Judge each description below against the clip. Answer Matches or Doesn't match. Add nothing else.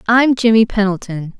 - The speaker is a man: Doesn't match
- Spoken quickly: Doesn't match